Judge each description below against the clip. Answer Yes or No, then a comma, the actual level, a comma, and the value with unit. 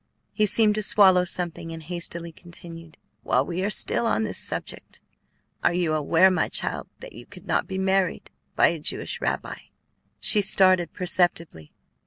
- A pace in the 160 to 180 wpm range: Yes, average, 165 wpm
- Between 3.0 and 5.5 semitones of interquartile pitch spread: No, narrow, 2.4 semitones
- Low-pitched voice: No, medium, 180 Hz